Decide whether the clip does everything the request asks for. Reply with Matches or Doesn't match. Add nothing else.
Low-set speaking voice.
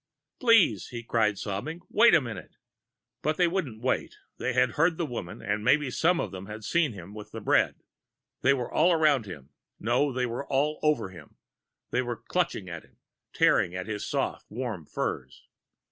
Matches